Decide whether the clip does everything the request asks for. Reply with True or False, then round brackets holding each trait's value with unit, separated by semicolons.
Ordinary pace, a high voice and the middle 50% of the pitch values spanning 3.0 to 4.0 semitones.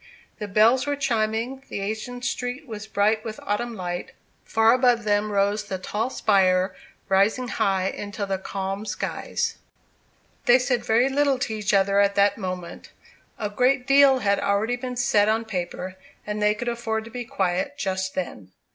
True (170 wpm; 215 Hz; 3.6 semitones)